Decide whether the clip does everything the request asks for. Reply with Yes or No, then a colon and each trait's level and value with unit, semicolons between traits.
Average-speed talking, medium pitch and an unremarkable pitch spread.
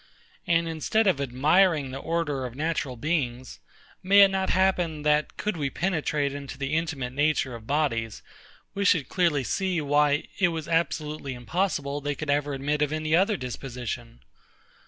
Yes: average, 160 wpm; medium, 150 Hz; average, 3.6 semitones